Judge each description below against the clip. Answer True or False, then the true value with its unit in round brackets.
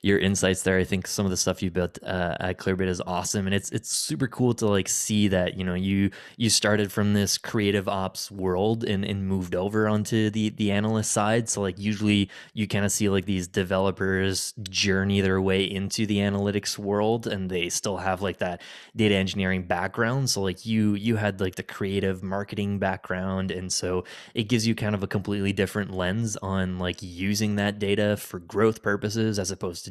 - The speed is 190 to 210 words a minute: True (205 wpm)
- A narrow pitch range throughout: True (1.9 semitones)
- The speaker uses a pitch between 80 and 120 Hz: True (100 Hz)